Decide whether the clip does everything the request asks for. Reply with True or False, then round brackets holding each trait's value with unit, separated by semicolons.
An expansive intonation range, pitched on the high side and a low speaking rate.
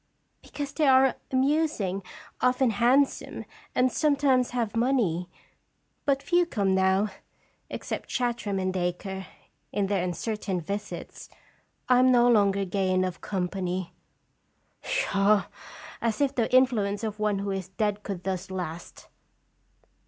False (5.0 semitones; 210 Hz; 130 wpm)